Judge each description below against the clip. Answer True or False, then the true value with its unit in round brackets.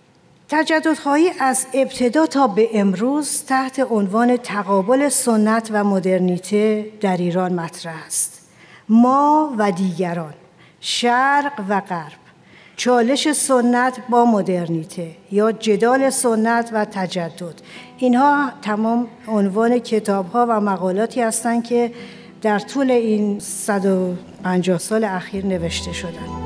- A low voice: False (215 Hz)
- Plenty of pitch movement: False (4.9 semitones)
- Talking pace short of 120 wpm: True (110 wpm)